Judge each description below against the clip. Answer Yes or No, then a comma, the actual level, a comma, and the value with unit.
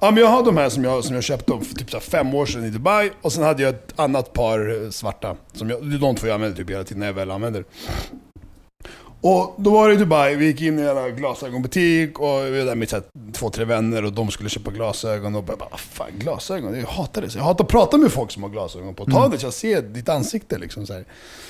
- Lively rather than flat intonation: Yes, wide, 6.2 semitones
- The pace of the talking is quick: Yes, fast, 255 wpm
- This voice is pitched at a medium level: No, low, 125 Hz